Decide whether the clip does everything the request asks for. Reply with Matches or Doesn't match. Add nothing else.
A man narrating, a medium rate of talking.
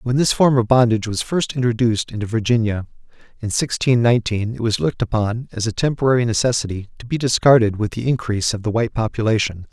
Matches